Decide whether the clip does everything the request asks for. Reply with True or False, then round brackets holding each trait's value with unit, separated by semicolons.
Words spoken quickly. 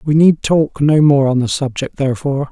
True (215 wpm)